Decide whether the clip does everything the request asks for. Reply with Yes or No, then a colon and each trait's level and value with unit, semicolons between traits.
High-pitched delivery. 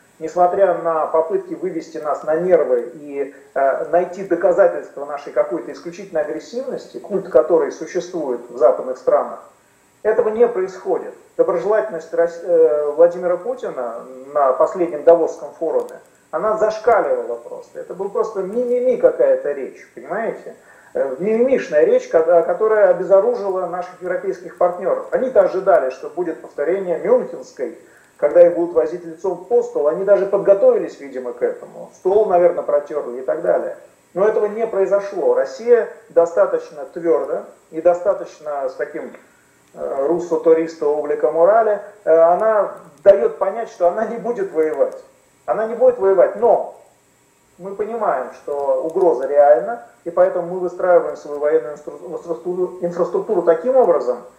Yes: high, 195 Hz